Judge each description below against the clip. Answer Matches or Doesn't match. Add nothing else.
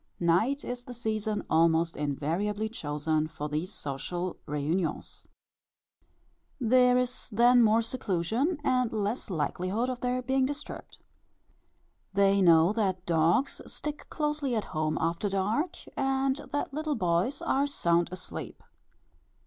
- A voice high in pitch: Matches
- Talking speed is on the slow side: Matches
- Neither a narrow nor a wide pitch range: Doesn't match